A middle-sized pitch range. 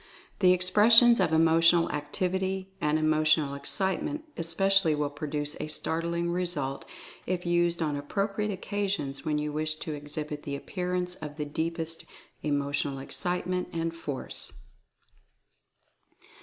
Yes: average, 3.4 semitones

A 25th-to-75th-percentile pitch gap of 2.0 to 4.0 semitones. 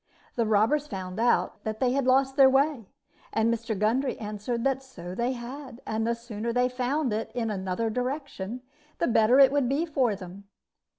Yes: average, 3.6 semitones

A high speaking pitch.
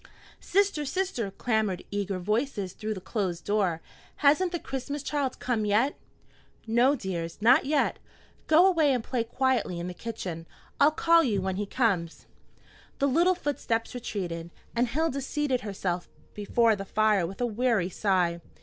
Yes: high, 225 Hz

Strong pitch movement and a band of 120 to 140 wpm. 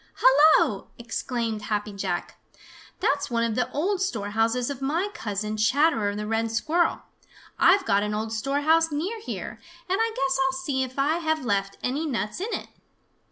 No: wide, 6.5 semitones; average, 165 wpm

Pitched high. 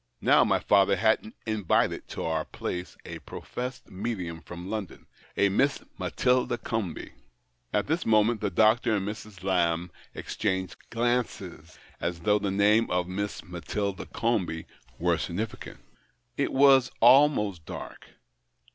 No: low, 105 Hz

